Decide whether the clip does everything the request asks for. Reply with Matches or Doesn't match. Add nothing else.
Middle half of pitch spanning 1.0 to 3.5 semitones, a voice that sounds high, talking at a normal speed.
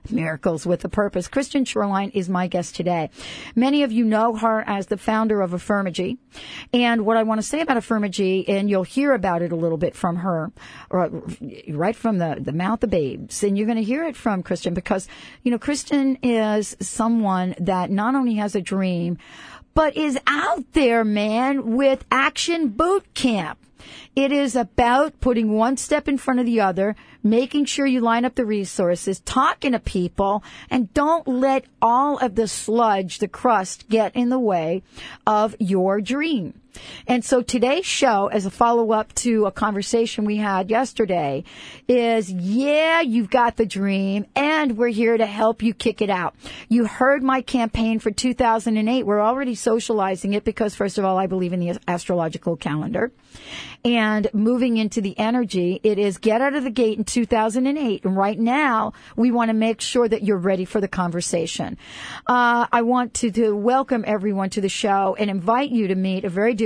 Doesn't match